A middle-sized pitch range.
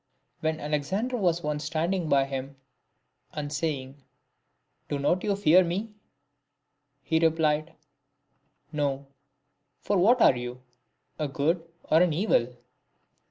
Yes: average, 3.6 semitones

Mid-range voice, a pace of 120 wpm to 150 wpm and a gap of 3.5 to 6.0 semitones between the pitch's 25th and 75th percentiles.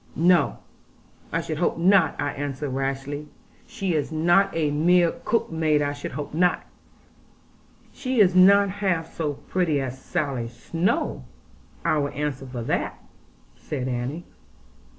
Yes: medium, 155 Hz; slow, 135 wpm; average, 4.1 semitones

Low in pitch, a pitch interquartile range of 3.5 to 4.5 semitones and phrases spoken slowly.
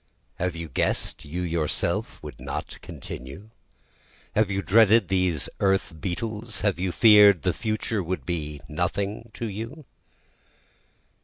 Yes: very low, 95 Hz; average, 3.9 semitones; slow, 130 wpm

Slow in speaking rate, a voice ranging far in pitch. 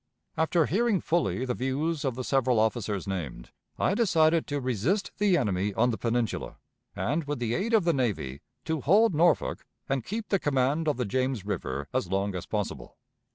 No: average, 185 wpm; wide, 7.0 semitones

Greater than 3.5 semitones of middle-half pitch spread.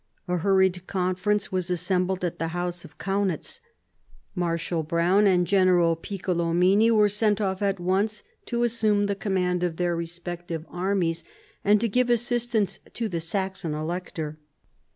No: average, 2.7 semitones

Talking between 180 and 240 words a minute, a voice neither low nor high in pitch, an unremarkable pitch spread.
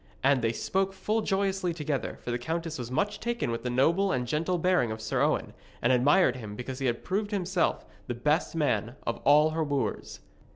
No: fast, 205 wpm; medium, 150 Hz; wide, 7.0 semitones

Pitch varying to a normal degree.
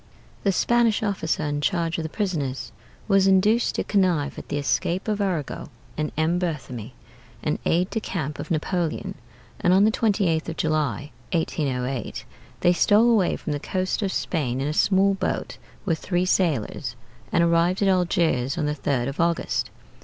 Yes: average, 4.4 semitones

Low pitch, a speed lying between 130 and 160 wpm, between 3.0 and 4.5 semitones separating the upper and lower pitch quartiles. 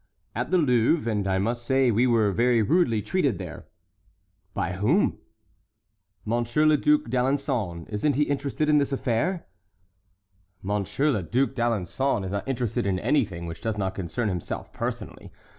No: low, 120 Hz; average, 155 wpm; average, 5.3 semitones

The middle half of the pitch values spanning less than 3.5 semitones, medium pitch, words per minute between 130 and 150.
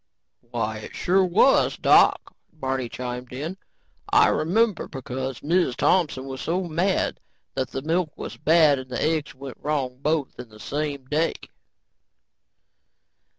No: average, 4.2 semitones; medium, 145 Hz; average, 140 wpm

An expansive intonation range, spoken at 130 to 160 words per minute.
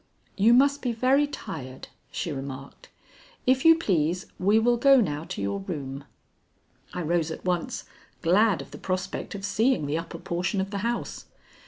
No: wide, 7.2 semitones; average, 170 wpm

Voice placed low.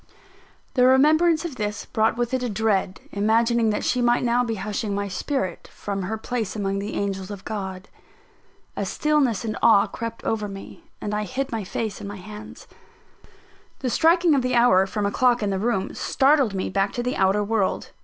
No: high, 220 Hz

